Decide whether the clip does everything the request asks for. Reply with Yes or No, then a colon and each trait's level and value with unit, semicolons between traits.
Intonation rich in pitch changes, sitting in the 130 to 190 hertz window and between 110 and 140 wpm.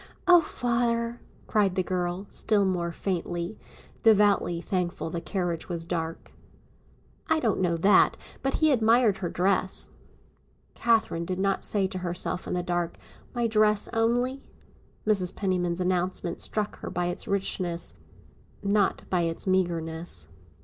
No: average, 3.5 semitones; medium, 185 Hz; slow, 135 wpm